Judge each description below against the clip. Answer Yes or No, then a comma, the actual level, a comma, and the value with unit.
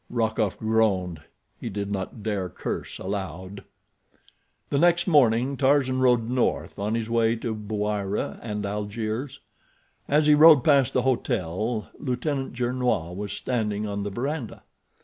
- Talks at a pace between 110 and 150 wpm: Yes, average, 140 wpm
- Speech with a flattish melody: No, average, 4.1 semitones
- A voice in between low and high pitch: No, low, 110 Hz